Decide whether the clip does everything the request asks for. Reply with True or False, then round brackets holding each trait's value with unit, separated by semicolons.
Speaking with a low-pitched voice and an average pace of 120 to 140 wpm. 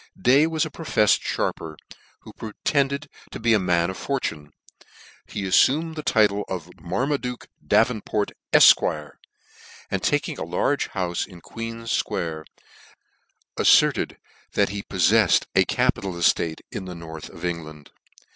True (100 Hz; 135 wpm)